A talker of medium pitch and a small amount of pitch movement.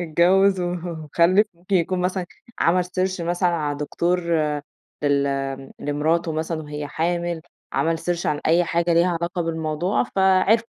Yes: medium, 170 Hz; narrow, 2.3 semitones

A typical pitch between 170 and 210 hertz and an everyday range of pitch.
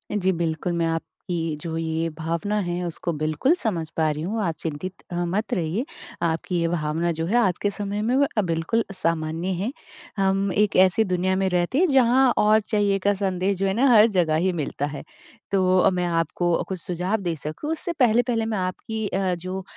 Yes: medium, 185 Hz; average, 3.9 semitones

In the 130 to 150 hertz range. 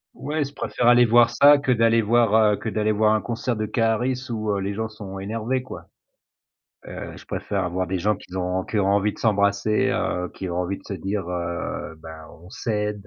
No: low, 105 Hz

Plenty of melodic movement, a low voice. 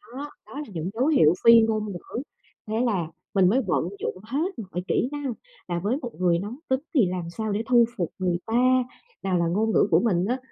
No: wide, 5.7 semitones; high, 215 Hz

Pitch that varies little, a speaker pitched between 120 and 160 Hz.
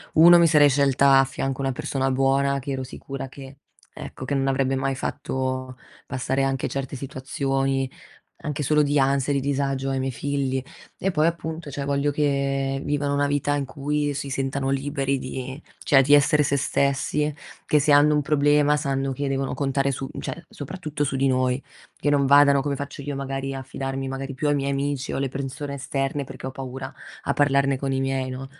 Yes: narrow, 1.2 semitones; low, 135 Hz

